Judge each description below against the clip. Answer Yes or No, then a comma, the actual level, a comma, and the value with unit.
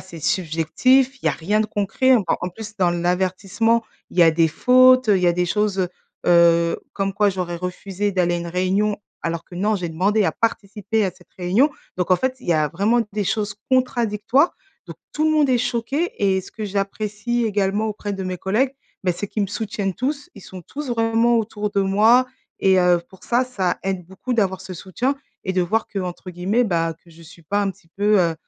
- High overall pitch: Yes, high, 200 Hz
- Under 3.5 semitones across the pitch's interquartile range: No, average, 3.9 semitones